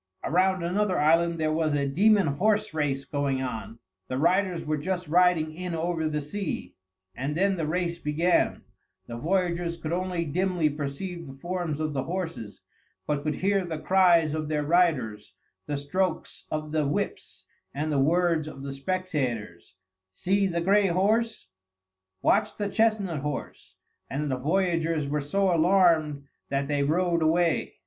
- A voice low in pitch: No, medium, 165 Hz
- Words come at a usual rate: Yes, average, 155 wpm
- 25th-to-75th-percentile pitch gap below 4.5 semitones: Yes, average, 3.7 semitones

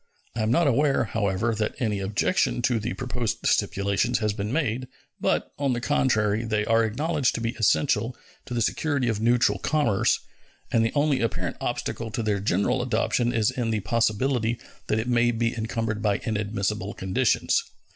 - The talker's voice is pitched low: Yes, low, 115 Hz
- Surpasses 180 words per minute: No, average, 175 wpm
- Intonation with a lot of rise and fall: No, narrow, 2.4 semitones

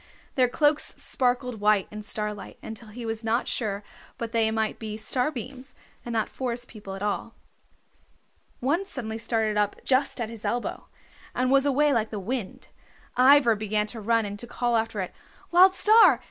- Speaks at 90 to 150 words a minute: No, average, 175 wpm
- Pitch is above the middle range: Yes, high, 230 Hz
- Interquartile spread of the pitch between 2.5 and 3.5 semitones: Yes, average, 3.1 semitones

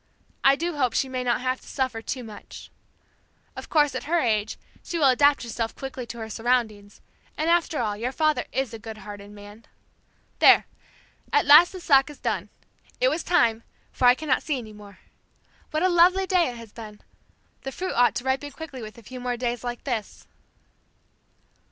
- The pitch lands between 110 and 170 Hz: No, very high, 255 Hz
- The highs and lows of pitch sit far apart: No, average, 4.8 semitones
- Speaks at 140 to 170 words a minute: No, average, 195 wpm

